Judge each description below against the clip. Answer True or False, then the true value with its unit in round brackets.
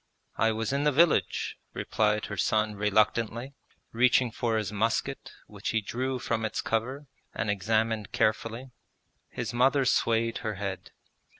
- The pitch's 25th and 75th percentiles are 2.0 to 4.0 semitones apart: True (2.5 semitones)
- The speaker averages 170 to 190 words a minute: False (140 wpm)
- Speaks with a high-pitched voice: False (115 Hz)